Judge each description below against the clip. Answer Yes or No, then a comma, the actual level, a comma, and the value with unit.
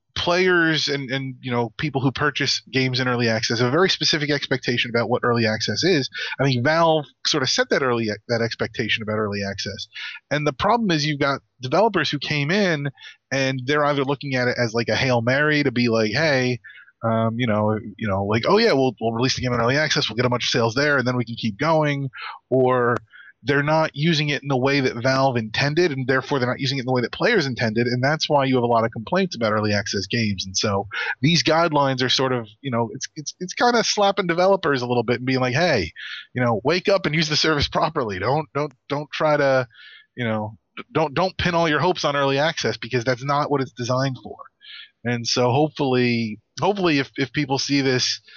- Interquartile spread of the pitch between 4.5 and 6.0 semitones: No, average, 3.9 semitones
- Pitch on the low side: Yes, low, 130 Hz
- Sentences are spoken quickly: Yes, fast, 235 wpm